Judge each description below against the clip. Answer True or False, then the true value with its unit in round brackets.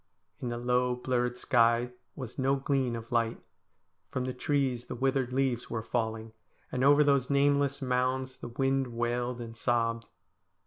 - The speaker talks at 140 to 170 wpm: True (155 wpm)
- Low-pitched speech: True (125 Hz)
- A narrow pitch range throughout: True (2.0 semitones)